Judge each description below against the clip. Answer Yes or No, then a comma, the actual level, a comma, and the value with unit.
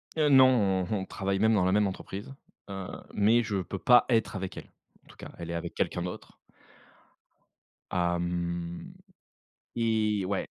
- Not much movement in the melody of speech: No, average, 3.6 semitones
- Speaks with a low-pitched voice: Yes, very low, 95 Hz